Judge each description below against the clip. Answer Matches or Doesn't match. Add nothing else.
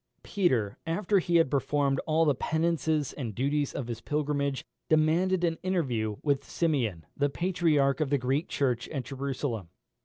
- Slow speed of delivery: Doesn't match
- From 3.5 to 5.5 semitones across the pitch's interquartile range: Matches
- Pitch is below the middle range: Doesn't match